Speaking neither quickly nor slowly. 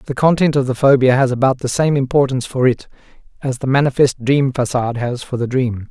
No: fast, 215 wpm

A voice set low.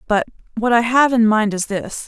No: high, 225 Hz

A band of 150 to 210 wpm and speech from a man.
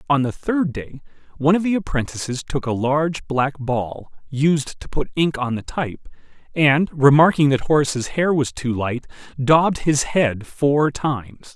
Yes: average, 170 wpm; male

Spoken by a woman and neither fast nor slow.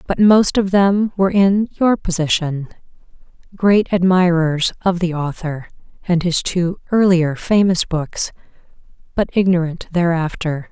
No: female; slow, 120 wpm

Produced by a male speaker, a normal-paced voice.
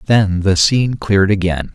Yes: male; average, 170 wpm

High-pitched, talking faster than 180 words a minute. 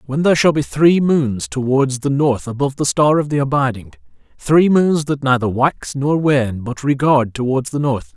No: low, 135 Hz; average, 200 wpm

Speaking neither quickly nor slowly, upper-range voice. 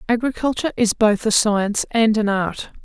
Yes: average, 170 wpm; high, 220 Hz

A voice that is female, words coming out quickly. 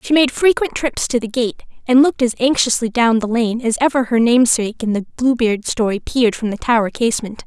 Yes: female; fast, 215 wpm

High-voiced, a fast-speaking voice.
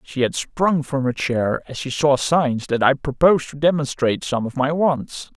No: medium, 140 Hz; fast, 210 wpm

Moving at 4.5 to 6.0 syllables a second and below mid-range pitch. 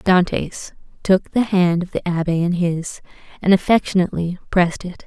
No: 5.0 syllables/s; medium, 180 Hz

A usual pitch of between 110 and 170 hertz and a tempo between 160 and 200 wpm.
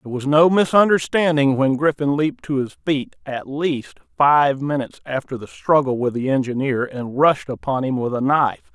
Yes: medium, 140 Hz; average, 185 wpm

